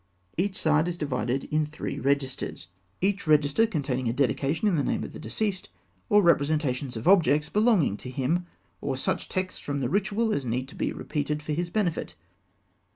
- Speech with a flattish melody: No, average, 5.2 semitones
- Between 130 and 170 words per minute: No, average, 180 wpm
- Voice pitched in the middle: Yes, medium, 150 Hz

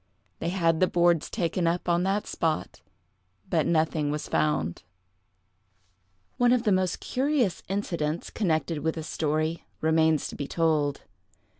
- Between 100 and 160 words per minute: Yes, average, 140 wpm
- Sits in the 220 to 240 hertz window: No, medium, 165 Hz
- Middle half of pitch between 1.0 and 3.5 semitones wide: Yes, average, 2.8 semitones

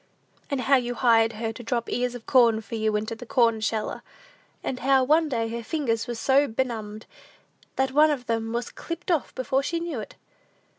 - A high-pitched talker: Yes, high, 240 Hz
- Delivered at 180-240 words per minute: Yes, average, 200 wpm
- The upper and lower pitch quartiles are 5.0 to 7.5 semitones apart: No, average, 3.0 semitones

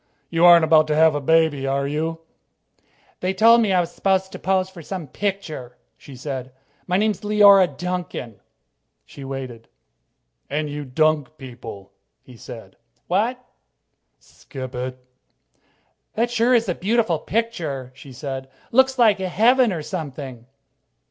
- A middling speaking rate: Yes, average, 155 wpm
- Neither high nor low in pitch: Yes, medium, 160 Hz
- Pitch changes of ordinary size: No, wide, 6.5 semitones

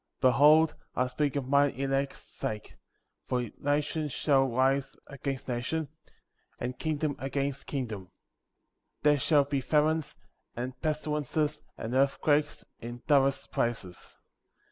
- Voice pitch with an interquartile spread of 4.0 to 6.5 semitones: No, narrow, 2.6 semitones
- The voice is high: No, medium, 140 Hz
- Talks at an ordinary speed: No, slow, 120 wpm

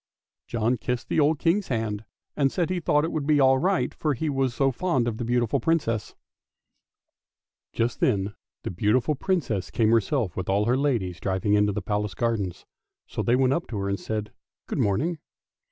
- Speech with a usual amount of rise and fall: No, wide, 5.7 semitones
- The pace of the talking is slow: No, average, 190 wpm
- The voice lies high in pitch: No, low, 120 Hz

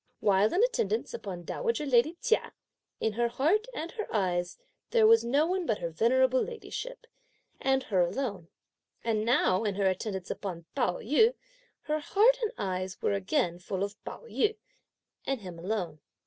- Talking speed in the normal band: Yes, average, 170 wpm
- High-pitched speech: Yes, high, 235 Hz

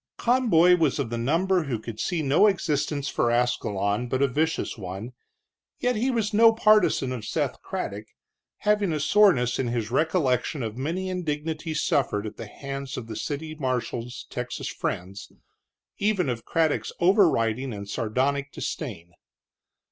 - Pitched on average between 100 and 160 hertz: Yes, medium, 140 Hz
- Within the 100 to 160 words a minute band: Yes, average, 150 wpm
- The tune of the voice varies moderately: No, wide, 6.8 semitones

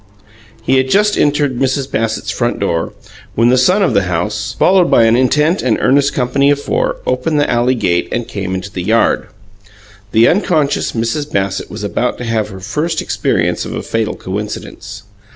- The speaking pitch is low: Yes, low, 120 Hz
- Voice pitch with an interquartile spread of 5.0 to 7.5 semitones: Yes, average, 5.3 semitones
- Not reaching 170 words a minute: No, average, 185 wpm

